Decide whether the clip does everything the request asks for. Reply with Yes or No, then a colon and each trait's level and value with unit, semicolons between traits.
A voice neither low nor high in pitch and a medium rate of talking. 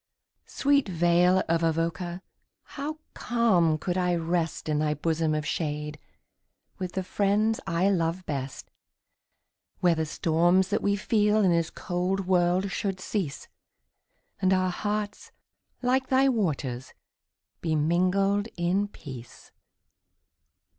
No: medium, 180 Hz; slow, 120 wpm